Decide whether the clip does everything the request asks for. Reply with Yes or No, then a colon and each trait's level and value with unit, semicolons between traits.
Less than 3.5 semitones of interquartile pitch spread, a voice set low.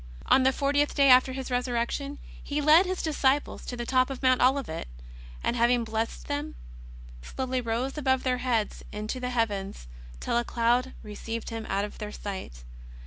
No: average, 2.8 semitones; very high, 250 Hz